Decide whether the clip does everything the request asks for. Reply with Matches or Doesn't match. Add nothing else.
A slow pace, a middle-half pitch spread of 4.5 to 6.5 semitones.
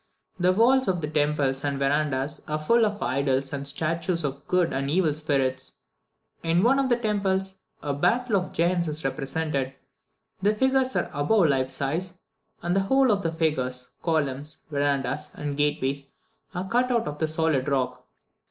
Doesn't match